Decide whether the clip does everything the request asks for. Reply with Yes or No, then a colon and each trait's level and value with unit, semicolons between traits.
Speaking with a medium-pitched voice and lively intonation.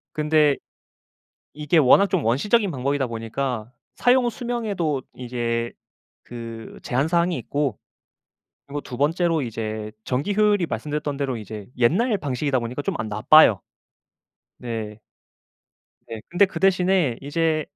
Yes: medium, 145 Hz; wide, 6.6 semitones